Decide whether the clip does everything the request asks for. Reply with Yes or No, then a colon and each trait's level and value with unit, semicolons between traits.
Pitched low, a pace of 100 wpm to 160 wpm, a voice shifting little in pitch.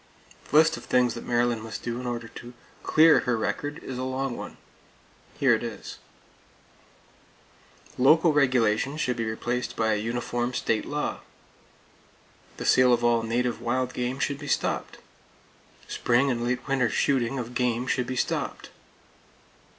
Yes: low, 125 Hz; average, 155 wpm; narrow, 1.9 semitones